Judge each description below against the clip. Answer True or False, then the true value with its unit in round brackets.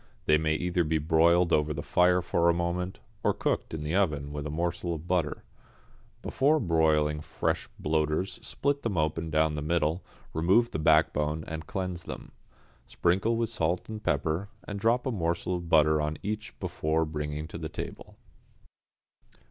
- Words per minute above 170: False (165 wpm)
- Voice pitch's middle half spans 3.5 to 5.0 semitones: False (2.8 semitones)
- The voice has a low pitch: True (80 Hz)